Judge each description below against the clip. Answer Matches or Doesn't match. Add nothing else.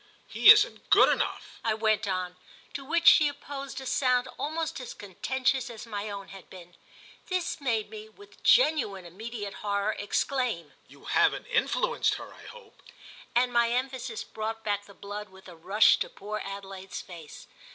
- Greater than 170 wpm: Doesn't match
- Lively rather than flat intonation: Doesn't match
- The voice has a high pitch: Matches